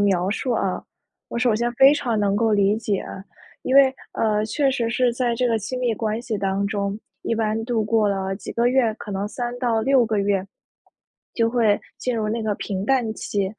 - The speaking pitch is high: Yes, high, 225 Hz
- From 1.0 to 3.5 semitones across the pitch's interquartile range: Yes, average, 2.9 semitones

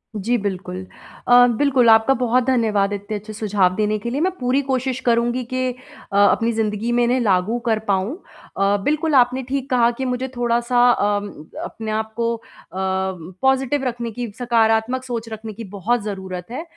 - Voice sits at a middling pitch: No, high, 235 Hz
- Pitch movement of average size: Yes, average, 3.3 semitones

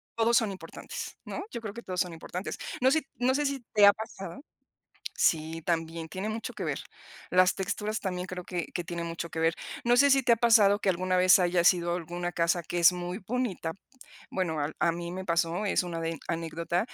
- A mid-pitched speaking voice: Yes, medium, 180 Hz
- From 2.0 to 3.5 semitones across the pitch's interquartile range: No, average, 3.9 semitones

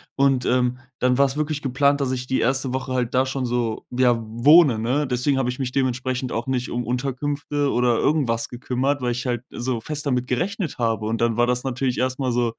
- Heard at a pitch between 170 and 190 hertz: No, low, 125 Hz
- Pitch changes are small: Yes, narrow, 2.0 semitones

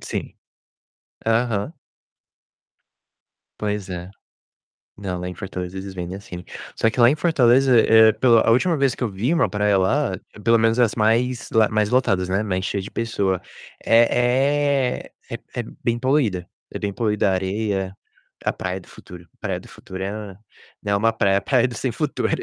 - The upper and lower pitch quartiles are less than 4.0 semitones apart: No, average, 4.3 semitones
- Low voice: Yes, low, 110 Hz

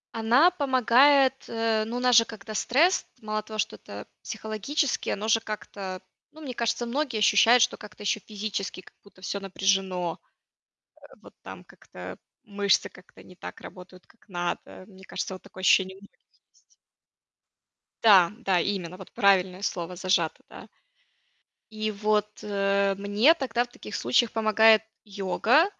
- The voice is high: Yes, high, 210 Hz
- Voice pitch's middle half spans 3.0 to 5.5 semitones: Yes, average, 3.3 semitones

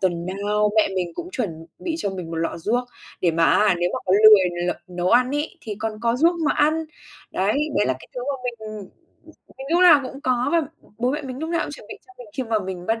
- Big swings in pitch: Yes, wide, 6.3 semitones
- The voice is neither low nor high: No, high, 215 Hz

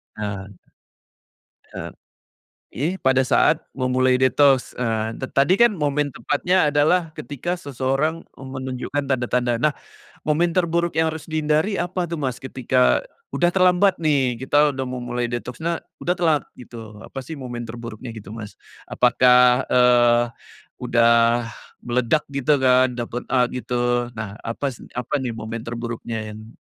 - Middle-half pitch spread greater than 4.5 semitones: No, average, 3.9 semitones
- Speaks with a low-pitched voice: Yes, low, 130 Hz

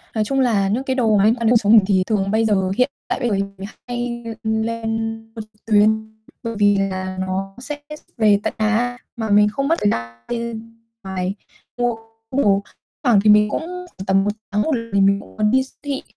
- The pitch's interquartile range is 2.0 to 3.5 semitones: Yes, average, 3.1 semitones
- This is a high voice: Yes, high, 220 Hz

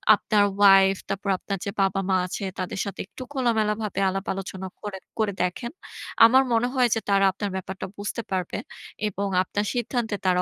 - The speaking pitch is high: Yes, high, 200 Hz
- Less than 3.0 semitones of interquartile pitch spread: Yes, narrow, 2.4 semitones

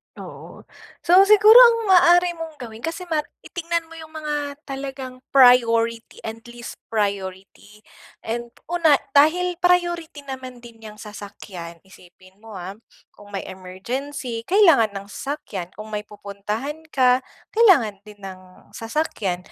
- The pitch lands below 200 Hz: No, very high, 250 Hz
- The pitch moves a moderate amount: No, wide, 7.6 semitones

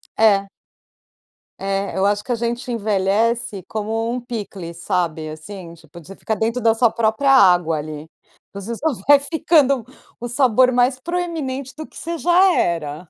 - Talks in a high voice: Yes, high, 220 Hz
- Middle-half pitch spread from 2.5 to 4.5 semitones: No, average, 5.2 semitones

